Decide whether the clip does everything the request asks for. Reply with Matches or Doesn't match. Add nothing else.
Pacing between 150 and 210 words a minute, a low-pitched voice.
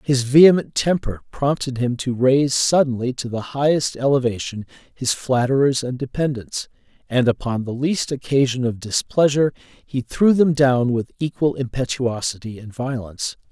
Doesn't match